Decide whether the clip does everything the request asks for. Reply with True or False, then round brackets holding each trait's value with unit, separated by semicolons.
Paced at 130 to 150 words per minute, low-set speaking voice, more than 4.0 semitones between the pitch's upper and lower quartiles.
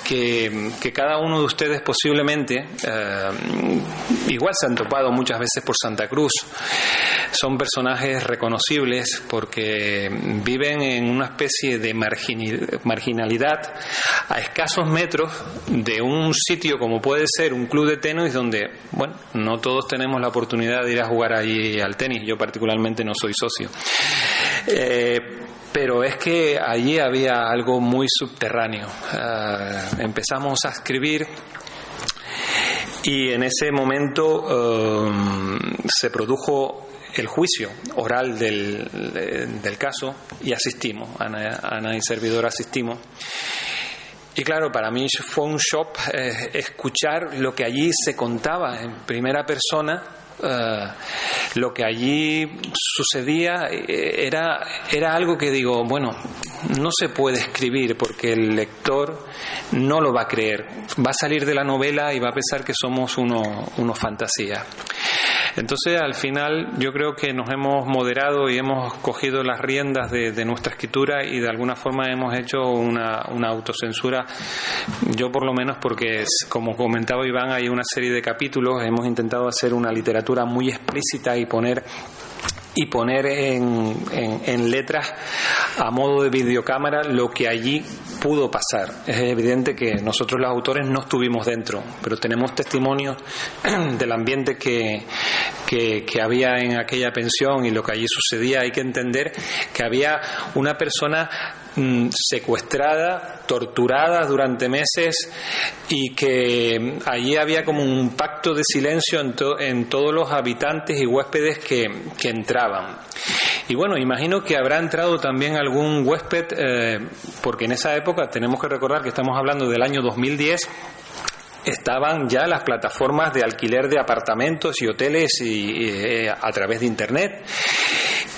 False (145 wpm; 130 Hz; 3.4 semitones)